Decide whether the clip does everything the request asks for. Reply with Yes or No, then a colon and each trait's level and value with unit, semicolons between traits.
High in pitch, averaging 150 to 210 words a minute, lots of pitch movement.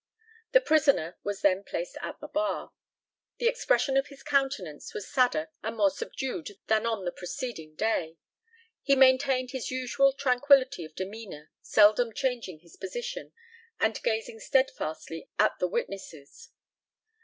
No: high, 230 Hz; average, 140 wpm; wide, 6.4 semitones